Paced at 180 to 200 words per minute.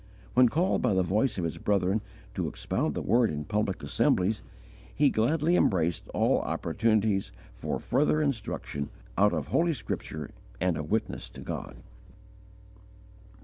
No: average, 145 wpm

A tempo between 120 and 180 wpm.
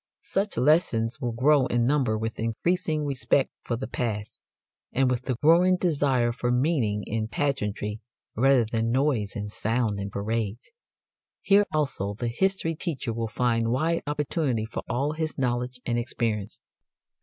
Yes: average, 150 wpm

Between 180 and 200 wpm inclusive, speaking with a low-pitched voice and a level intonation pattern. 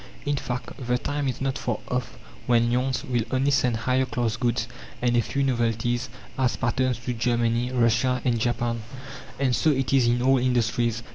Yes: average, 185 wpm; low, 125 Hz; narrow, 1.7 semitones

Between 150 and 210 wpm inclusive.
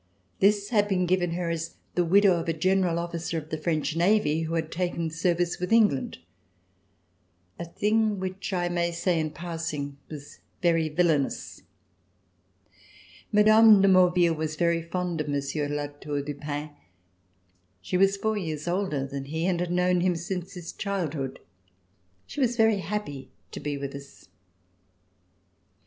Yes: average, 160 wpm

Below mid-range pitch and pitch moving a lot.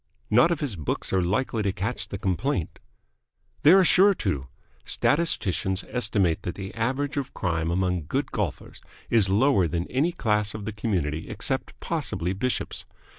Yes: low, 105 Hz; wide, 6.4 semitones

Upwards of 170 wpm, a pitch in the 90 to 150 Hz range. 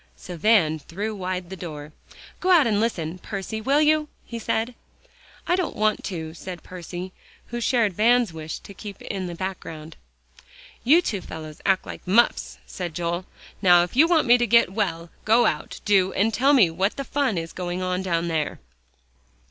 No: average, 185 wpm; high, 190 Hz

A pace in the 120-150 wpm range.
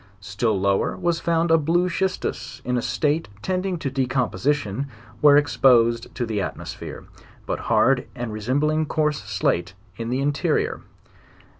Yes: average, 140 wpm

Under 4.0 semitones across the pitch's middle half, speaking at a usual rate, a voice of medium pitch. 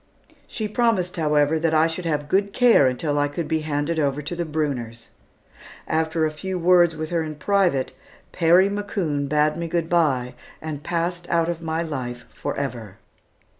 Yes: average, 2.9 semitones; average, 170 wpm; medium, 160 Hz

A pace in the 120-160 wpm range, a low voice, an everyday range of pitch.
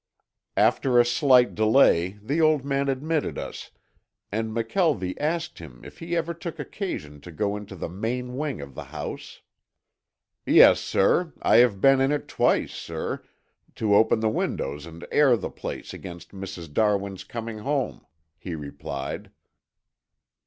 No: average, 145 wpm; low, 115 Hz; wide, 6.9 semitones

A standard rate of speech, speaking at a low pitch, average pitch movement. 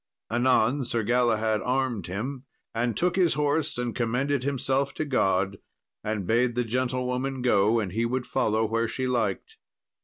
Yes: average, 155 wpm; low, 125 Hz; average, 3.0 semitones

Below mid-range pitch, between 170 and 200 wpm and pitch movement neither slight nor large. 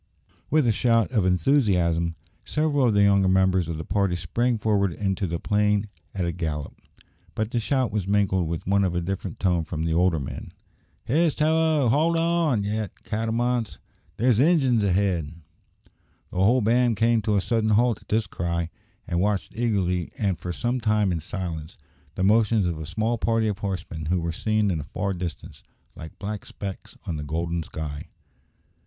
Yes: low, 100 Hz; average, 180 wpm; average, 4.7 semitones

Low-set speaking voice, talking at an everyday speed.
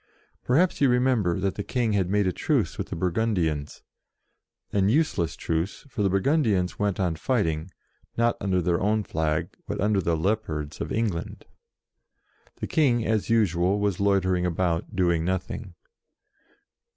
Yes: very low, 95 Hz; average, 150 wpm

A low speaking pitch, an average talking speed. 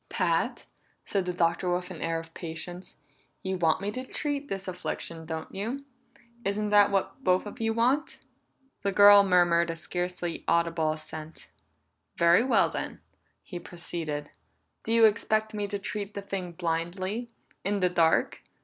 No: medium, 185 Hz; average, 160 wpm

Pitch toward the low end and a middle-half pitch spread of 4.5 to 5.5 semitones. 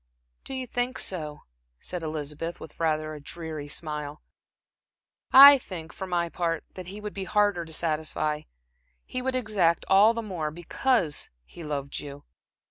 No: medium, 170 Hz; average, 5.1 semitones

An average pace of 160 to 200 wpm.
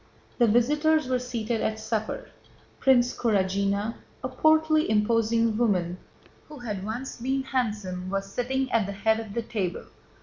No: average, 145 wpm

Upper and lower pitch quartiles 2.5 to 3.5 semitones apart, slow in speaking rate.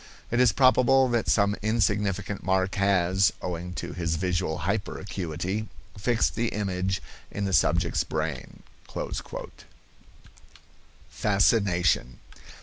Yes: average, 3.0 semitones; slow, 100 wpm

